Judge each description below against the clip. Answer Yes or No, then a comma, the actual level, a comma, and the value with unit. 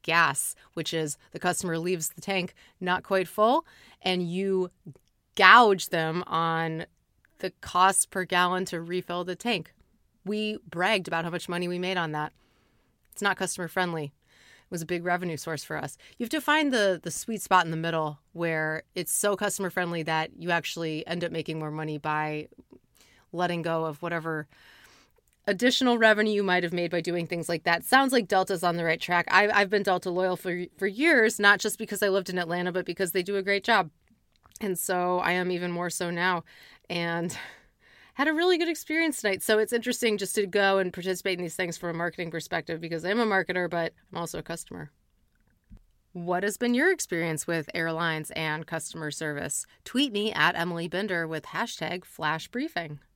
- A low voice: No, medium, 180 Hz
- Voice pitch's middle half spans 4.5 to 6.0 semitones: No, average, 3.0 semitones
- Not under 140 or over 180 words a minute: No, average, 195 wpm